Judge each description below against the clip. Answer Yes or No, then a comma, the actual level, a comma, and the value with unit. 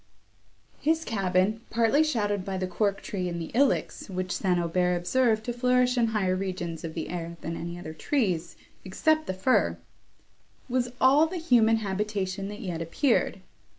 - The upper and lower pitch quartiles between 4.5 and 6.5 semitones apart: Yes, average, 5.2 semitones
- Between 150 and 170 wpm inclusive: Yes, average, 165 wpm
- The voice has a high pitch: Yes, high, 200 Hz